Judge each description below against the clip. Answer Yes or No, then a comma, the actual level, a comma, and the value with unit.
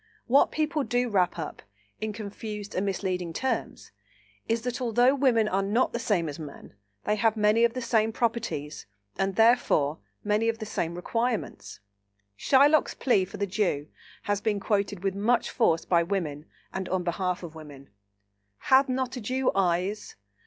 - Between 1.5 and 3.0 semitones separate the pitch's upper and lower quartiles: No, average, 4.6 semitones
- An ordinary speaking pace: Yes, average, 165 wpm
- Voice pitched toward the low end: No, high, 210 Hz